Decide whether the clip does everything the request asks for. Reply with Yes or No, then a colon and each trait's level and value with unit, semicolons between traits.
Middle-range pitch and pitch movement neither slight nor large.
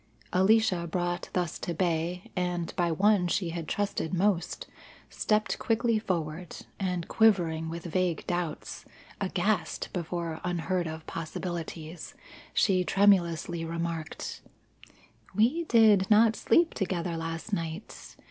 Yes: medium, 175 Hz; average, 3.1 semitones